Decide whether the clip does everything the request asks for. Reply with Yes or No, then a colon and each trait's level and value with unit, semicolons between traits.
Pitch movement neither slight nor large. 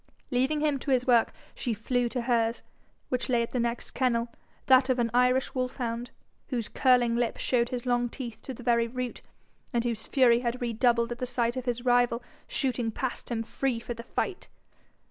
No: narrow, 1.4 semitones